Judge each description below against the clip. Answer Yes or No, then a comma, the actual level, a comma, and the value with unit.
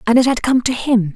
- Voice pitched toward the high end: Yes, high, 240 Hz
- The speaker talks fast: Yes, fast, 315 wpm